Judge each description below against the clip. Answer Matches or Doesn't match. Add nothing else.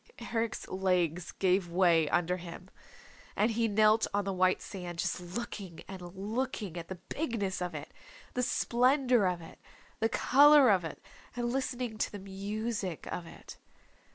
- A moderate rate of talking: Matches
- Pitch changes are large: Doesn't match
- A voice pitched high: Matches